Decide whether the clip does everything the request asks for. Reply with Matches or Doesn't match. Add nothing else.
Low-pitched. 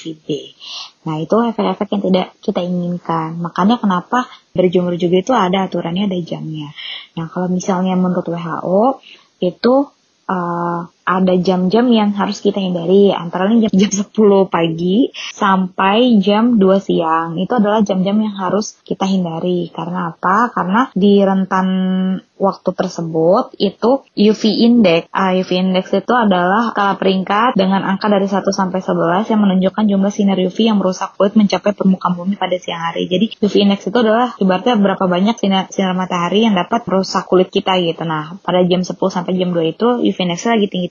Doesn't match